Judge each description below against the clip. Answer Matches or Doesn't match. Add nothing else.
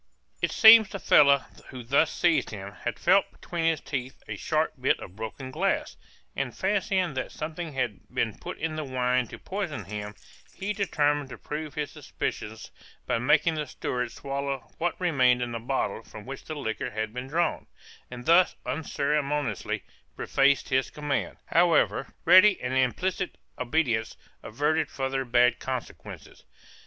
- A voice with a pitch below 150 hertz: Matches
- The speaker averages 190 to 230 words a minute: Doesn't match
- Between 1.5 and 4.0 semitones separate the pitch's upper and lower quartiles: Doesn't match